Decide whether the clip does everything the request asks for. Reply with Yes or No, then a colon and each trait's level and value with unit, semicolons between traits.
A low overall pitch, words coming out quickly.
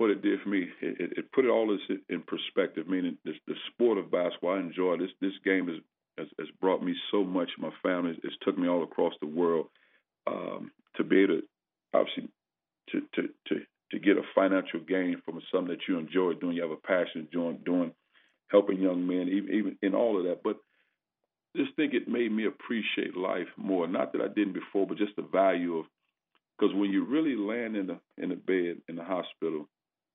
Yes: low, 100 Hz; fast, 215 wpm